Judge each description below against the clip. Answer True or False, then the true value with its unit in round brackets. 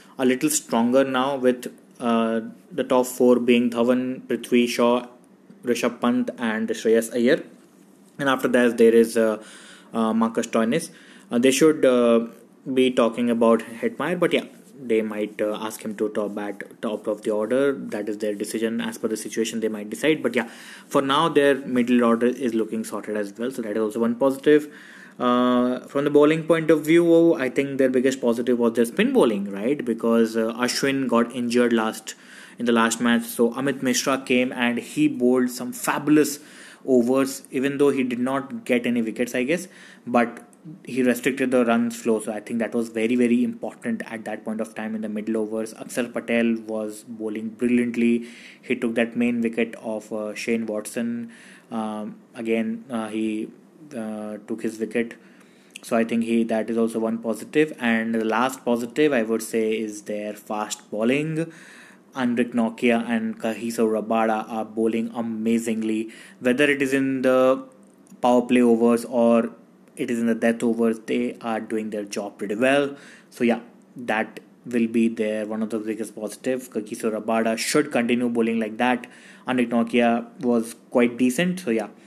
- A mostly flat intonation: True (2.2 semitones)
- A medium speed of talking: True (180 wpm)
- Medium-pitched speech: False (120 Hz)